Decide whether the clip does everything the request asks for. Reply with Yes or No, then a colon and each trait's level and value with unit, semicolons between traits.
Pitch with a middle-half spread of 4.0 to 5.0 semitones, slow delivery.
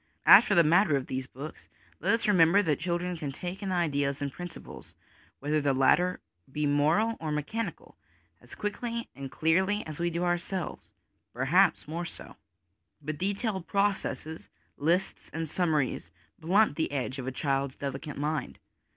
No: average, 4.6 semitones; average, 160 wpm